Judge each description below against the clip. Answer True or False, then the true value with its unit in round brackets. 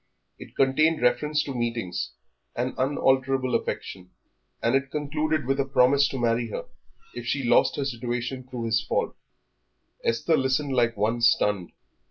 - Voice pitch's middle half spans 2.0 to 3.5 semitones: True (2.7 semitones)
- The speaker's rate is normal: True (150 wpm)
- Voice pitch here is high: False (130 Hz)